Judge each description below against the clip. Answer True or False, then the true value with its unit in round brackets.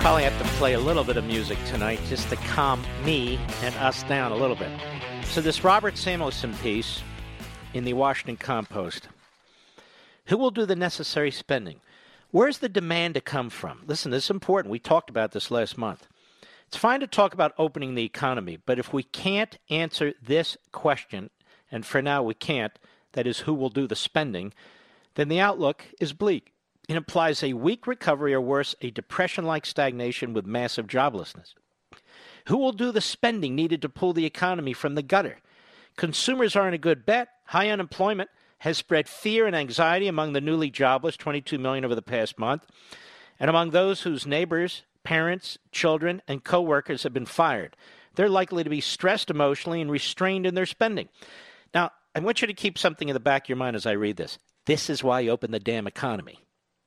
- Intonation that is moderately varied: False (6.4 semitones)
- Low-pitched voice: False (155 Hz)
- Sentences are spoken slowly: False (190 wpm)